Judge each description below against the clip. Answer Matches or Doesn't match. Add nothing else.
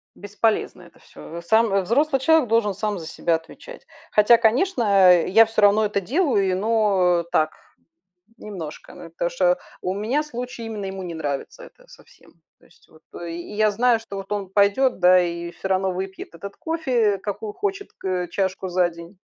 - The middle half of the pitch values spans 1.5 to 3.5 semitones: Doesn't match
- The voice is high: Matches